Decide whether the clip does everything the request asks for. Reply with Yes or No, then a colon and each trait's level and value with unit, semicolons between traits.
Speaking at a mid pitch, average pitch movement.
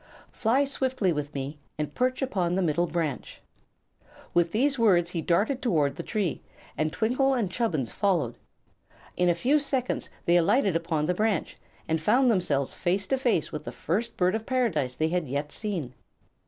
No: medium, 180 Hz; wide, 7.0 semitones